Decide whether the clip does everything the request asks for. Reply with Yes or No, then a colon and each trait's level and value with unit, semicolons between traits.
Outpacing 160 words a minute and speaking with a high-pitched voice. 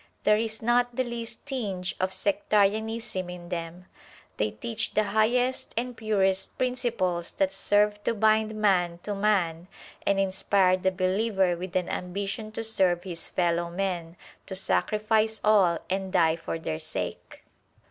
No: average, 145 wpm; high, 195 Hz